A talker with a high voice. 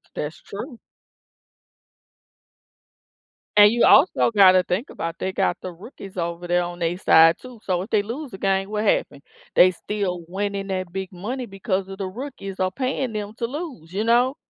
Yes: high, 195 Hz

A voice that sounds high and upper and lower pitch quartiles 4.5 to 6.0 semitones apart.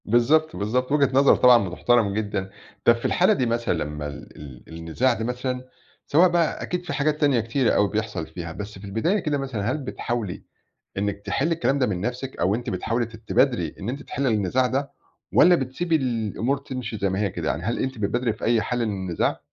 No: low, 120 Hz; average, 4.9 semitones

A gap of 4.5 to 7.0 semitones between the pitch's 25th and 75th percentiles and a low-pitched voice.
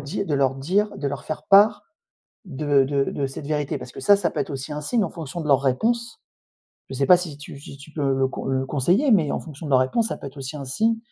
No: average, 5.0 semitones; medium, 145 Hz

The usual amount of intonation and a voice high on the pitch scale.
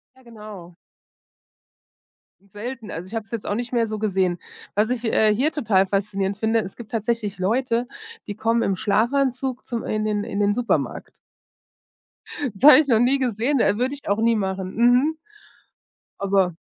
Yes: average, 3.3 semitones; high, 220 Hz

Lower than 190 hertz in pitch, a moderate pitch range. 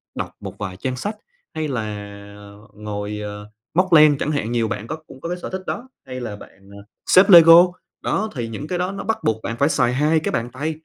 No: low, 135 Hz; wide, 7.1 semitones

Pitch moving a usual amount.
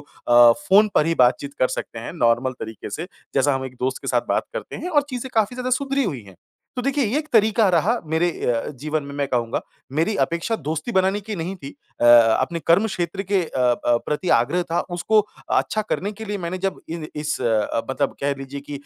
No: wide, 7.5 semitones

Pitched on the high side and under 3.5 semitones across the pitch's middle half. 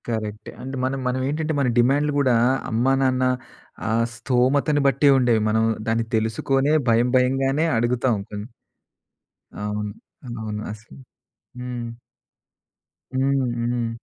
No: low, 125 Hz; average, 3.0 semitones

